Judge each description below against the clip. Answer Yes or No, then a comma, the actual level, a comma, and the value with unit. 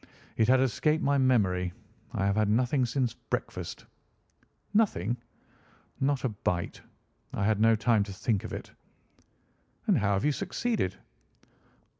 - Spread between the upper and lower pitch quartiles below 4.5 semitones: No, average, 5.1 semitones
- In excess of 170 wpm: No, average, 140 wpm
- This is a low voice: Yes, low, 115 Hz